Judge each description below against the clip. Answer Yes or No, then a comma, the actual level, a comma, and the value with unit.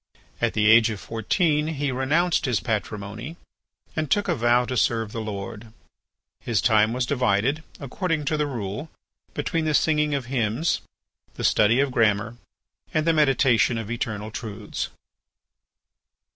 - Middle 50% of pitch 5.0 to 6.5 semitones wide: Yes, average, 5.3 semitones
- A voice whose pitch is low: Yes, low, 120 Hz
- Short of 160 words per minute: Yes, average, 145 wpm